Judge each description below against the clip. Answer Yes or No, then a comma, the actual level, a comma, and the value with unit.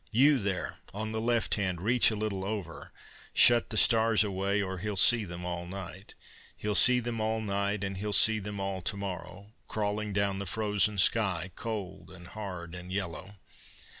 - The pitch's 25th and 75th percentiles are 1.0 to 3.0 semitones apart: Yes, narrow, 2.5 semitones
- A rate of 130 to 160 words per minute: No, average, 180 wpm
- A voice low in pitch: Yes, low, 100 Hz